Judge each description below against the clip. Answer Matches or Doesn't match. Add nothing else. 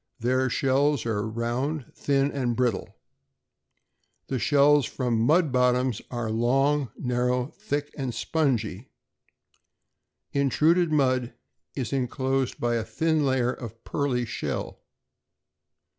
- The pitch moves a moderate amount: Matches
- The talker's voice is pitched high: Doesn't match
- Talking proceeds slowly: Matches